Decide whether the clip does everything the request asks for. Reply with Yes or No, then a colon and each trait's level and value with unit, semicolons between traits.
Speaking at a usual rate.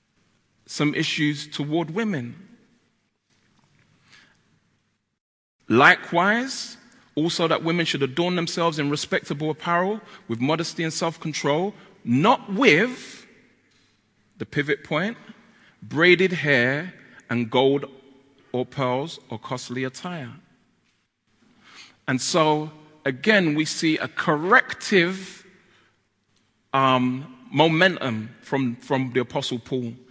No: slow, 95 wpm